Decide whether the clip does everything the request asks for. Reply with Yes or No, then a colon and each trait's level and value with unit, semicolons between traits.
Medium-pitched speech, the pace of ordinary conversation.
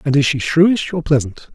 No: medium, 150 Hz; fast, 235 wpm